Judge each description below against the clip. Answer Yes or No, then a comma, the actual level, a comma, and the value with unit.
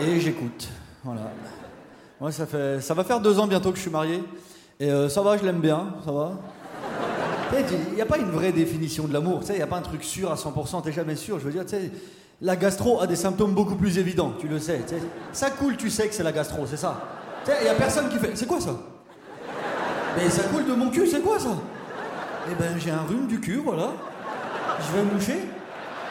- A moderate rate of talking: No, fast, 255 wpm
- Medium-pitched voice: Yes, medium, 180 Hz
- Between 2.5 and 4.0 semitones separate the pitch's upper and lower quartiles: No, average, 4.4 semitones